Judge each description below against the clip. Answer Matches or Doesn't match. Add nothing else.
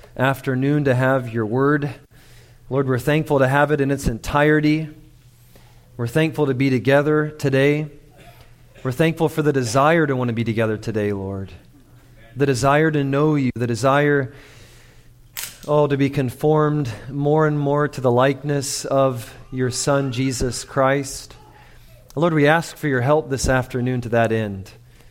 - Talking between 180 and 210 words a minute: Doesn't match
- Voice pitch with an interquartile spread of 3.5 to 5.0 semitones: Doesn't match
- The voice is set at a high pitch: Doesn't match